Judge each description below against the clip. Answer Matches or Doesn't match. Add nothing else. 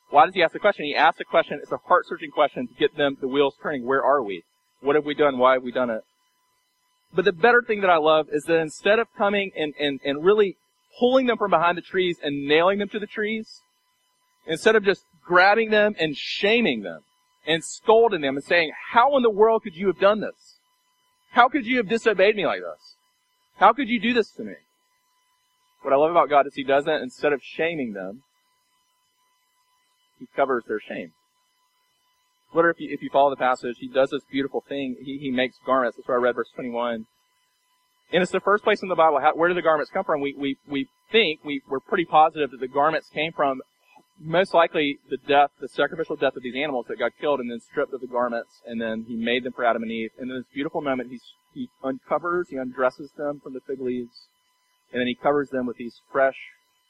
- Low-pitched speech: Doesn't match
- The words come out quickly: Matches